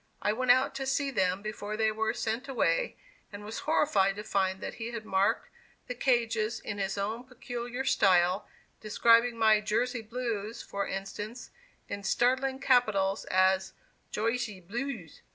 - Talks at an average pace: Yes, average, 155 wpm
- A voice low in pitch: No, high, 220 Hz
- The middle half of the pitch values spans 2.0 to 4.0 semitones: Yes, average, 3.6 semitones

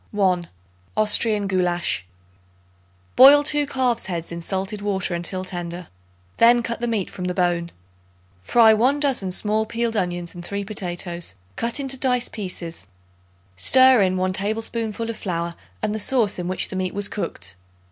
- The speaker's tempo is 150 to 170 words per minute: Yes, average, 160 wpm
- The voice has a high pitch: Yes, high, 200 Hz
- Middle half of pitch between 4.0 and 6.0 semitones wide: Yes, average, 4.6 semitones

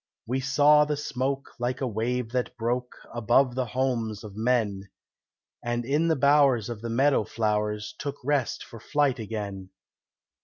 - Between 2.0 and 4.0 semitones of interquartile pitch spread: Yes, average, 3.7 semitones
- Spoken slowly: No, average, 155 wpm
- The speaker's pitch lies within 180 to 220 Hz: No, low, 125 Hz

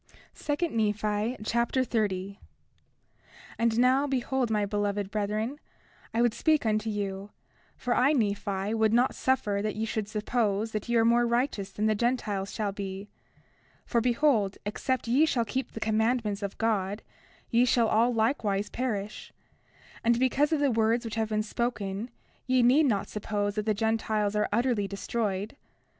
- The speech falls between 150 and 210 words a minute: Yes, average, 160 wpm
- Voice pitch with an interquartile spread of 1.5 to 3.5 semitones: Yes, average, 2.7 semitones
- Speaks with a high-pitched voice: Yes, high, 220 Hz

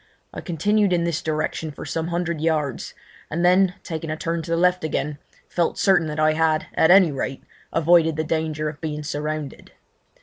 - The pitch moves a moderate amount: No, narrow, 1.9 semitones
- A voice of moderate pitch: Yes, medium, 160 Hz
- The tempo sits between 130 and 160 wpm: No, average, 190 wpm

